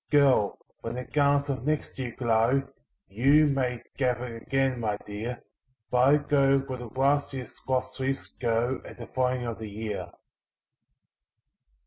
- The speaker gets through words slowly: No, average, 150 wpm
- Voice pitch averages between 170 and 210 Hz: No, low, 130 Hz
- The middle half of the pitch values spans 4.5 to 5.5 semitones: No, average, 2.7 semitones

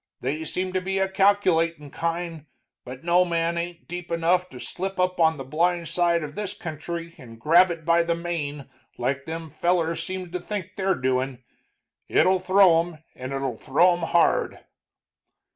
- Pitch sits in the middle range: Yes, medium, 170 Hz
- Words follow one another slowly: No, average, 175 wpm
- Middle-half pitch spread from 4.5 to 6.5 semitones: No, average, 2.9 semitones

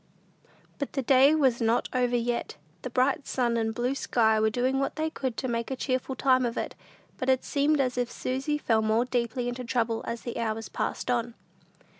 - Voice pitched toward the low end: No, high, 245 Hz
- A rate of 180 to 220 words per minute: Yes, fast, 205 wpm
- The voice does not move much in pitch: Yes, narrow, 2.2 semitones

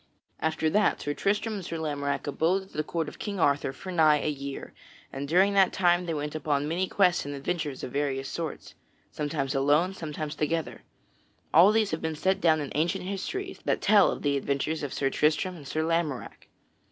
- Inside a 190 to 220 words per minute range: Yes, average, 200 wpm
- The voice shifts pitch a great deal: No, average, 3.9 semitones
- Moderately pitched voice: Yes, medium, 155 Hz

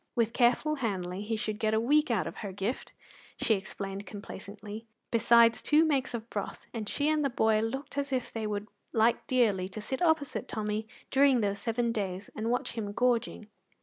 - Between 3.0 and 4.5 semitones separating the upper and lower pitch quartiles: Yes, average, 3.4 semitones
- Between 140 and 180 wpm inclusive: No, average, 190 wpm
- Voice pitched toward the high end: Yes, high, 225 Hz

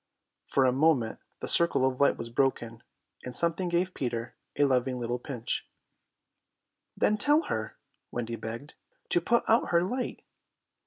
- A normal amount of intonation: No, wide, 6.3 semitones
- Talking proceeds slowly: No, average, 150 wpm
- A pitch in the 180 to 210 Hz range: No, low, 130 Hz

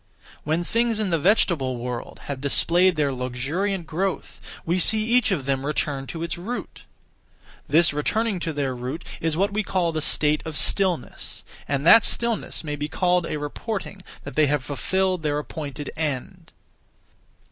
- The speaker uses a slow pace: No, average, 165 wpm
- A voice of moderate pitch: Yes, medium, 160 Hz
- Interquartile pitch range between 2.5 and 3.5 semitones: No, average, 4.7 semitones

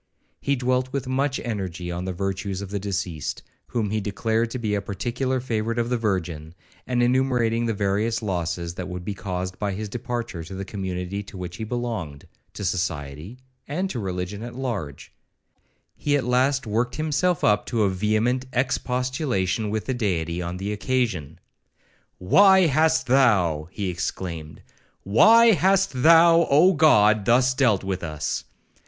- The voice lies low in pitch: Yes, low, 110 Hz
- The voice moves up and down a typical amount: No, wide, 5.7 semitones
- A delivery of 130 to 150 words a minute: No, average, 160 wpm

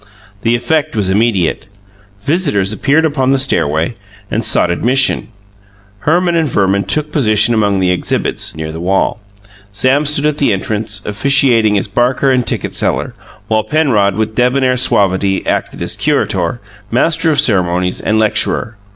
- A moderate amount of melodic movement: No, wide, 5.7 semitones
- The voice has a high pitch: No, low, 115 Hz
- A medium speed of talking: Yes, average, 150 wpm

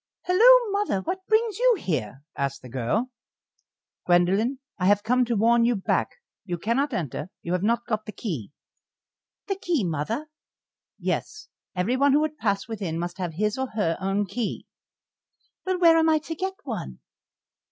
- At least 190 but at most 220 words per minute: No, average, 165 wpm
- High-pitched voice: Yes, high, 225 Hz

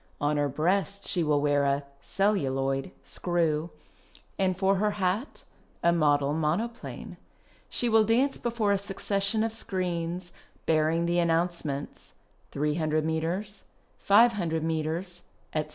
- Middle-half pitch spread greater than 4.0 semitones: Yes, average, 4.5 semitones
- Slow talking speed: Yes, slow, 120 wpm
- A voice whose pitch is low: No, medium, 170 Hz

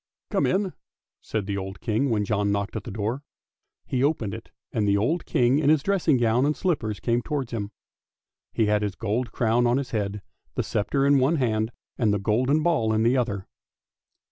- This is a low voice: Yes, low, 115 Hz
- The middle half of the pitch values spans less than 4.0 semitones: No, average, 4.8 semitones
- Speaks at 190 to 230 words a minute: Yes, fast, 205 wpm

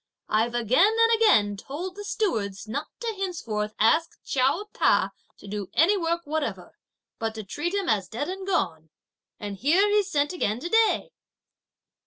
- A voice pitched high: Yes, very high, 295 Hz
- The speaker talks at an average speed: Yes, average, 165 wpm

